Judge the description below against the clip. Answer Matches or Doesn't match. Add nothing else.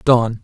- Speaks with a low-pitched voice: Matches